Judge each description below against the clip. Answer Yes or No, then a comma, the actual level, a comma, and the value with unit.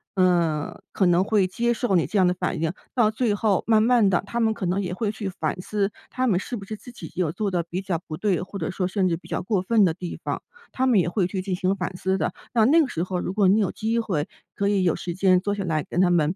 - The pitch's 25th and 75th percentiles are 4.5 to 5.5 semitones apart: No, average, 3.2 semitones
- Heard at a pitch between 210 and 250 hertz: No, high, 190 Hz